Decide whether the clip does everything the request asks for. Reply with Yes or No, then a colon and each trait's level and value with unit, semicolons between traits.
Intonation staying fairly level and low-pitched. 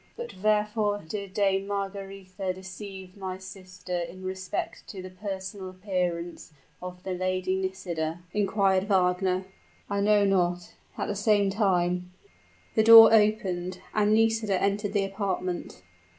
No: narrow, 1.9 semitones; high, 190 Hz